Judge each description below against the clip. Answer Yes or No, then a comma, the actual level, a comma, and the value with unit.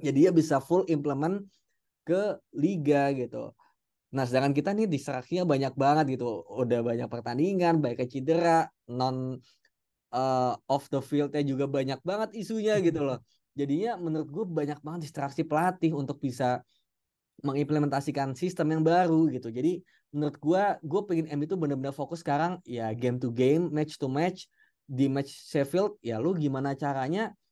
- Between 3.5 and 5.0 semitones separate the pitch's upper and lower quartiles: Yes, average, 3.8 semitones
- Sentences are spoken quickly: Yes, fast, 155 wpm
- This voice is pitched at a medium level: Yes, medium, 145 Hz